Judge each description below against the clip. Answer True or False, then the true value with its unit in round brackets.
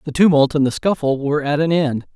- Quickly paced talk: True (250 wpm)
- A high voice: False (150 Hz)